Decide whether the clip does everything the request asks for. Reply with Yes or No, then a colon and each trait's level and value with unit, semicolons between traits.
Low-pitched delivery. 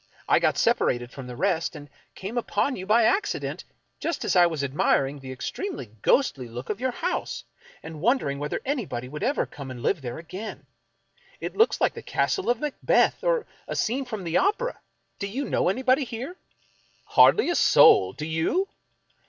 No: high, 195 Hz